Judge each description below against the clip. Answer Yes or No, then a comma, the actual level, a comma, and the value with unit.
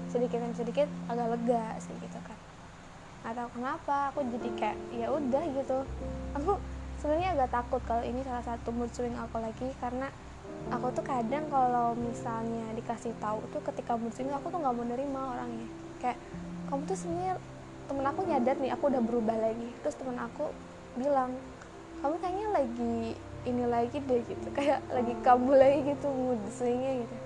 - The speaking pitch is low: No, high, 245 Hz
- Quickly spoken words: Yes, fast, 170 wpm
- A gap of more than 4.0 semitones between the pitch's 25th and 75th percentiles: No, average, 3.0 semitones